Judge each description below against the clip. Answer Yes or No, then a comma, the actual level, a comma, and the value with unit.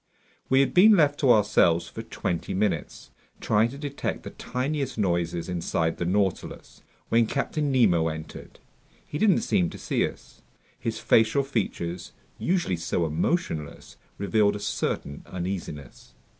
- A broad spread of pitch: Yes, wide, 8.1 semitones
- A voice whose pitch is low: Yes, low, 105 Hz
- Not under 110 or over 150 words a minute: Yes, average, 140 wpm